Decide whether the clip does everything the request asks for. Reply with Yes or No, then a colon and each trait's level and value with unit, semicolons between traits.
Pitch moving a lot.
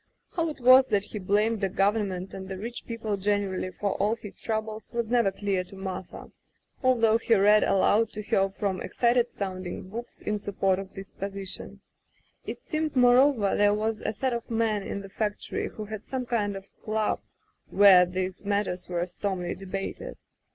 No: average, 2.7 semitones